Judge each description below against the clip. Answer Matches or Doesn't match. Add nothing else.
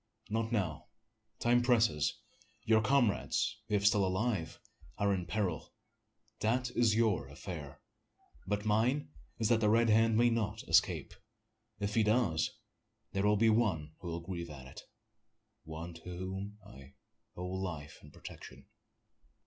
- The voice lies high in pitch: Doesn't match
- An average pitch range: Matches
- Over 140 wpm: Doesn't match